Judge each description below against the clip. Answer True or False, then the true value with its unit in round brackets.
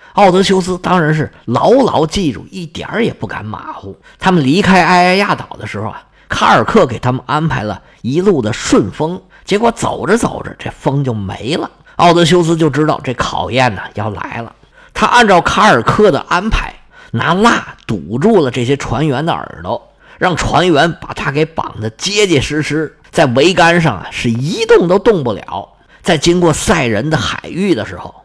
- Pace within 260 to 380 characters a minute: True (270 characters per minute)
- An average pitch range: False (6.1 semitones)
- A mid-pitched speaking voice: True (155 Hz)